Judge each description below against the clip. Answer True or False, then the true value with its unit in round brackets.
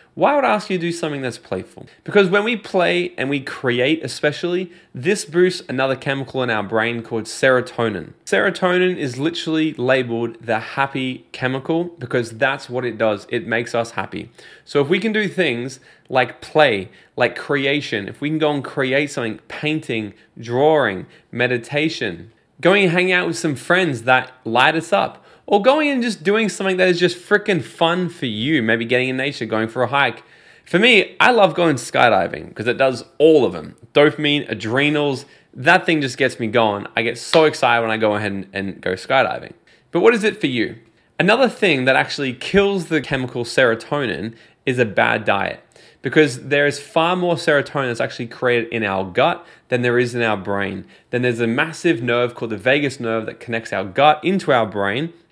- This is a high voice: False (135 Hz)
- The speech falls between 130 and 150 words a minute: False (195 wpm)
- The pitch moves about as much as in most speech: False (6.0 semitones)